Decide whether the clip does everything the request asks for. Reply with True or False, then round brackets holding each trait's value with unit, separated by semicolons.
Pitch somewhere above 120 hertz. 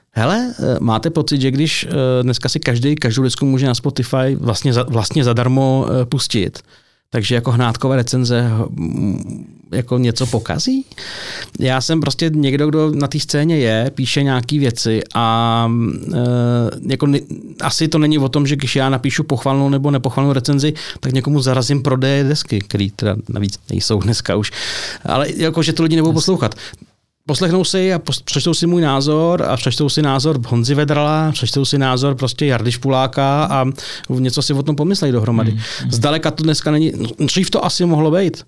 True (135 Hz)